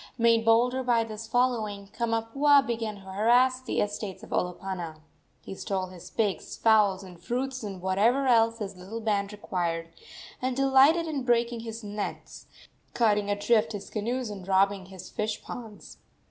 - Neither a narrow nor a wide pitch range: Yes, average, 3.4 semitones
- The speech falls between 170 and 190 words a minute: No, average, 155 wpm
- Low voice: No, high, 220 Hz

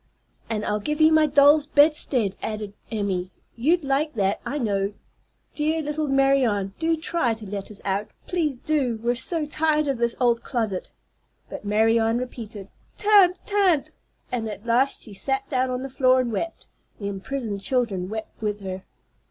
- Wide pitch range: Yes, wide, 6.0 semitones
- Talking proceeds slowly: No, average, 170 wpm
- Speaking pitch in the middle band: No, high, 245 Hz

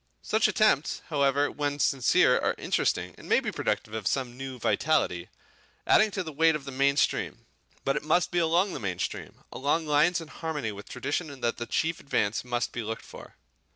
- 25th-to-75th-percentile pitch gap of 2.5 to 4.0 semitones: No, average, 4.7 semitones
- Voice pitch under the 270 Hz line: Yes, medium, 140 Hz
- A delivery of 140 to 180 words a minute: No, average, 195 wpm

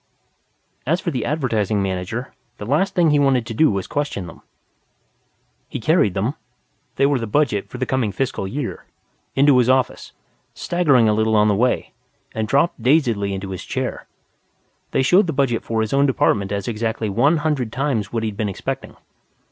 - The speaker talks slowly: No, average, 180 wpm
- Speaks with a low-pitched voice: Yes, low, 120 Hz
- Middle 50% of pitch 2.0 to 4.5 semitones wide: No, average, 5.1 semitones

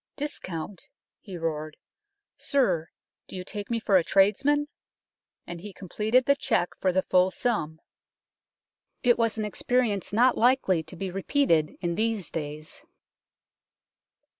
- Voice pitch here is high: Yes, high, 195 Hz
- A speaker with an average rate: Yes, average, 150 wpm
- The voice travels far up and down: Yes, wide, 5.7 semitones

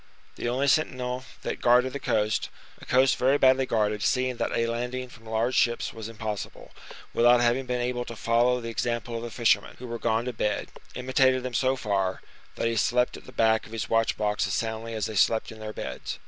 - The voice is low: Yes, low, 120 Hz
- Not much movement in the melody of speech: Yes, narrow, 2.2 semitones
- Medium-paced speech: No, fast, 220 wpm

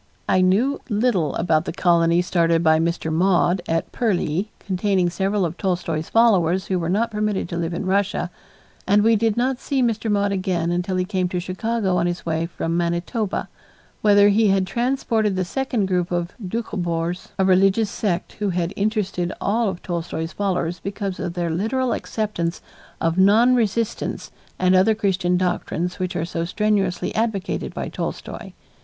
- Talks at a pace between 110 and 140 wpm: No, average, 170 wpm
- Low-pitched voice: No, medium, 185 Hz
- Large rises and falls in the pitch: No, average, 3.3 semitones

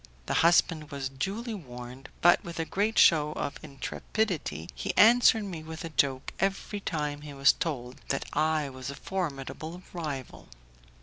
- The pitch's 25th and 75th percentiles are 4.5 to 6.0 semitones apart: Yes, average, 4.8 semitones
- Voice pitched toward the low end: No, medium, 155 Hz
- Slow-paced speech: No, average, 150 wpm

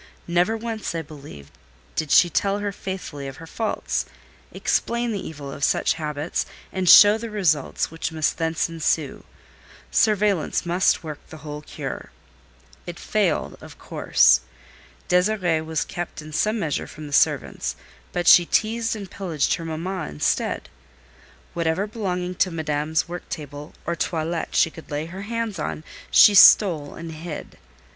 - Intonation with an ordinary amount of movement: Yes, average, 4.2 semitones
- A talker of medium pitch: Yes, medium, 170 Hz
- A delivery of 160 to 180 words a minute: No, average, 150 wpm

